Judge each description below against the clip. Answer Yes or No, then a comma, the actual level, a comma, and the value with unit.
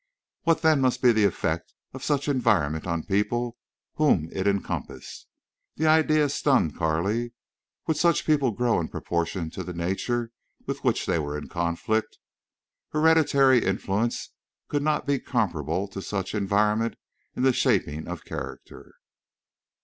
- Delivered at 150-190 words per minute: No, average, 140 wpm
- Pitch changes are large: Yes, wide, 7.7 semitones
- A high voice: No, low, 110 Hz